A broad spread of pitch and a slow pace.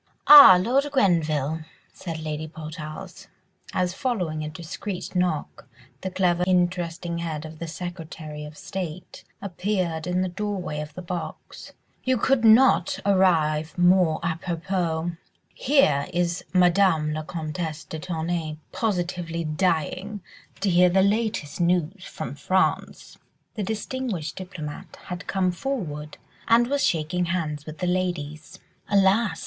No: average, 3.3 semitones; slow, 130 wpm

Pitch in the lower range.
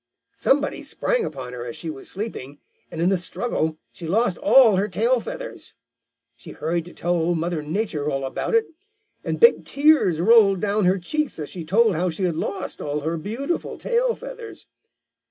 No: medium, 185 Hz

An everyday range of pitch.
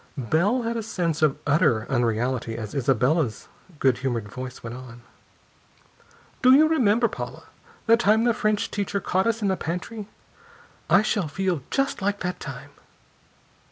No: wide, 8.9 semitones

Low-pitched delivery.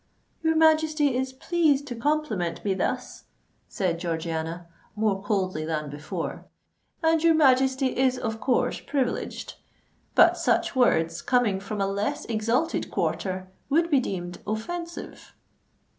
No: high, 235 Hz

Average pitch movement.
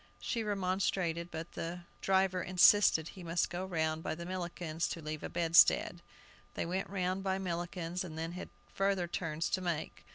No: narrow, 2.1 semitones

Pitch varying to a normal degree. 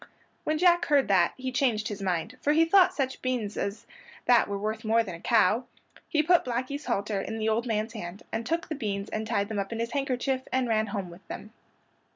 Yes: average, 4.3 semitones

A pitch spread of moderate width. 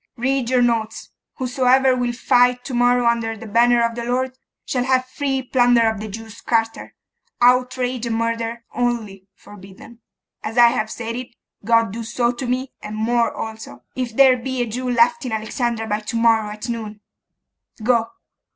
No: narrow, 1.9 semitones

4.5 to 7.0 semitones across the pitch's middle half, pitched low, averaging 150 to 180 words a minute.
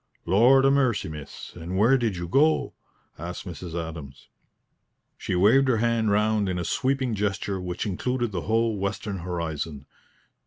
Yes: average, 5.1 semitones; low, 100 Hz; average, 155 wpm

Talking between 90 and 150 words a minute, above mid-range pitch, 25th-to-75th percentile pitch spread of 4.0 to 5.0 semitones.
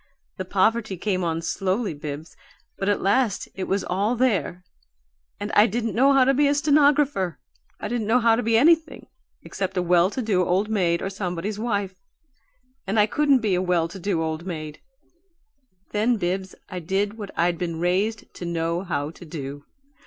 No: average, 185 wpm; high, 195 Hz; average, 4.4 semitones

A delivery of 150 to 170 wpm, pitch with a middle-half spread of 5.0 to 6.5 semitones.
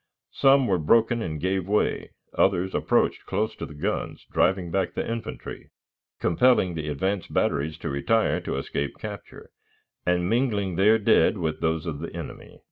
Yes: average, 160 wpm; wide, 5.4 semitones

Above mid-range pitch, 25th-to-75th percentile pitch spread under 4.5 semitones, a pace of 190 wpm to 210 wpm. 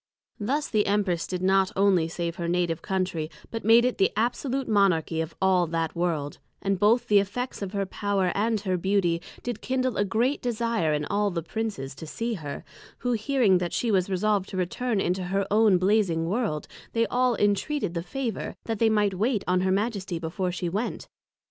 Yes: high, 195 Hz; average, 4.1 semitones; average, 200 wpm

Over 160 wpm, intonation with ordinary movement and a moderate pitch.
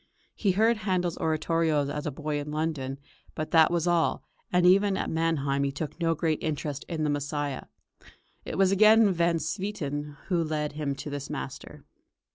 Yes: average, 175 wpm; average, 3.3 semitones; medium, 160 Hz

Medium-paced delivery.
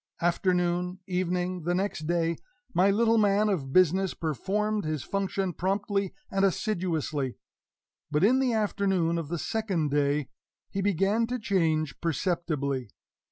No: slow, 130 wpm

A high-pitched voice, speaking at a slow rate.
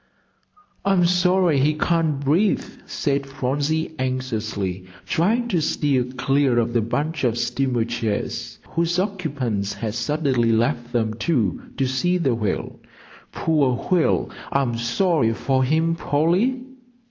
No: low, 135 Hz; slow, 125 wpm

